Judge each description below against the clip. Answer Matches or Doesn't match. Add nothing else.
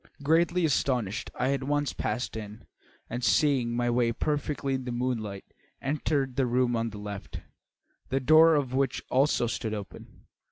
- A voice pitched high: Doesn't match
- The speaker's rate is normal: Matches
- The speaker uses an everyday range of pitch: Matches